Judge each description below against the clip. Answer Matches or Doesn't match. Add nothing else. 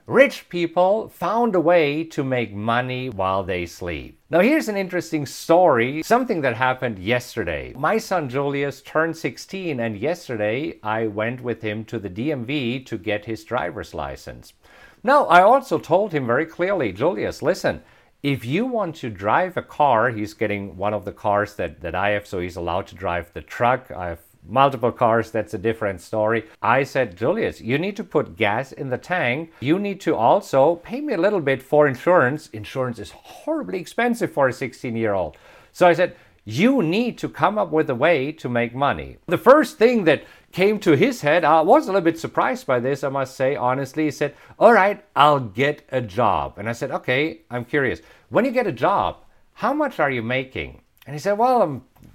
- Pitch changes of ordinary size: Doesn't match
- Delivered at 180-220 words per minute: Matches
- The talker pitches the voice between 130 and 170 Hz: Matches